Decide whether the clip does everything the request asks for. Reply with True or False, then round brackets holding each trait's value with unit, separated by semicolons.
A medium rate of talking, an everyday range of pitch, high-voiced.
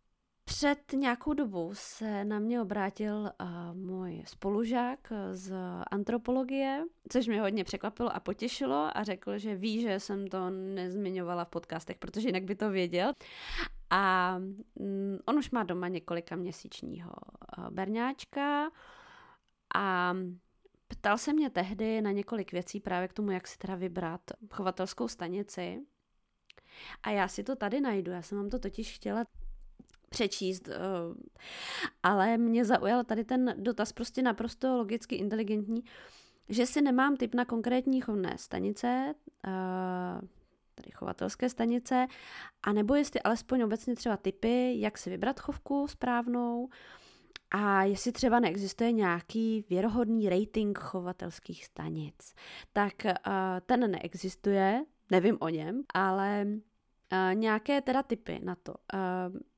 True (125 wpm; 4.6 semitones; 210 Hz)